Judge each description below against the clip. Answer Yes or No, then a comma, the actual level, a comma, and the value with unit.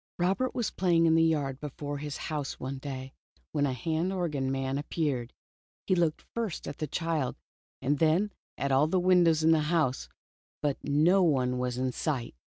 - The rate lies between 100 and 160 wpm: No, average, 180 wpm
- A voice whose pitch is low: No, medium, 150 Hz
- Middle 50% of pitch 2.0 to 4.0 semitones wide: Yes, average, 3.7 semitones